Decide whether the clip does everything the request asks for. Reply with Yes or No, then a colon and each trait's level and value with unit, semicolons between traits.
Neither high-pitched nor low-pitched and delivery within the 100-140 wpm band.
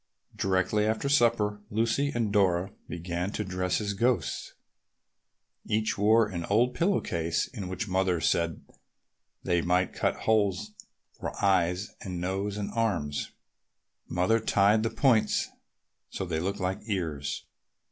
No: low, 100 Hz; slow, 135 wpm